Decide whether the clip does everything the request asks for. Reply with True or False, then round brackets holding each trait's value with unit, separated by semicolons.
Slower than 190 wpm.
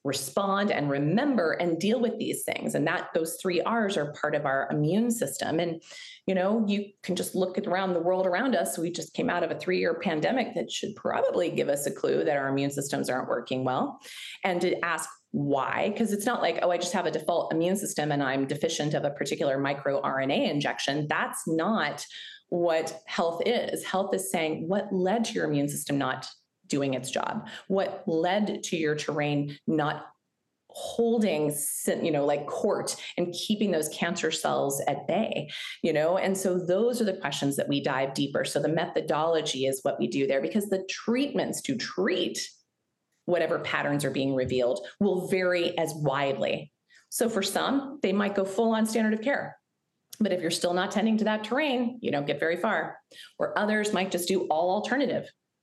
False (195 wpm)